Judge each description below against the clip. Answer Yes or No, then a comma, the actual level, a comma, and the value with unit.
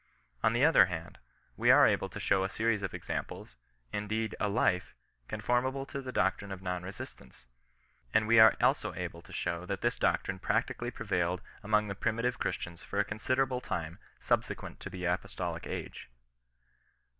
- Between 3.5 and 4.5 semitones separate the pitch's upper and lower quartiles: Yes, average, 4.2 semitones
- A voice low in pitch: Yes, low, 100 Hz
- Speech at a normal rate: Yes, average, 170 wpm